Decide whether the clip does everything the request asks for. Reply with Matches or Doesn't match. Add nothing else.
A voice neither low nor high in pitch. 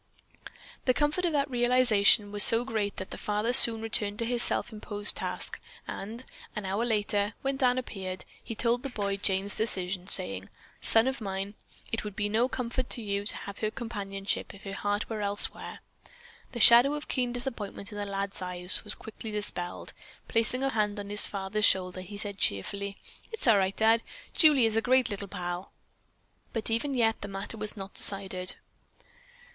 Doesn't match